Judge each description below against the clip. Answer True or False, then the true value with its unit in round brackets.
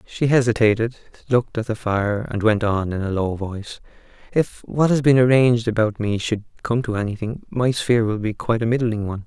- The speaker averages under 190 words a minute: False (205 wpm)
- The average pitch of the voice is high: False (115 Hz)